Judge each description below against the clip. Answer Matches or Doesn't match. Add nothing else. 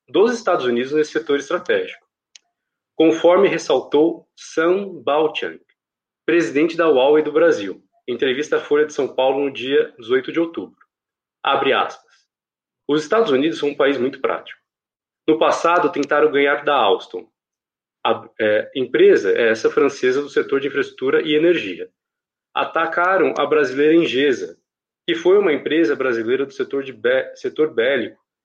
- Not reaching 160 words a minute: Matches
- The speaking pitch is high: Matches